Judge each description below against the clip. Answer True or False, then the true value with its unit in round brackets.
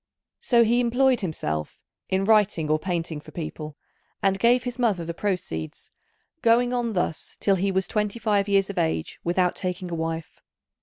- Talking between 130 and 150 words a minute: False (170 wpm)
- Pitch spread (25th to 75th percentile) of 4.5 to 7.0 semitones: True (5.5 semitones)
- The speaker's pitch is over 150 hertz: True (190 Hz)